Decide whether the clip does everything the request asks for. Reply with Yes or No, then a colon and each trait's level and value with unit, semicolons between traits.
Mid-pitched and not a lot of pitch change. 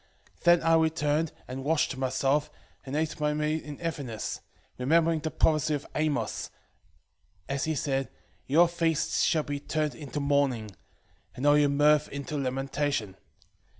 Yes: medium, 145 Hz; narrow, 2.3 semitones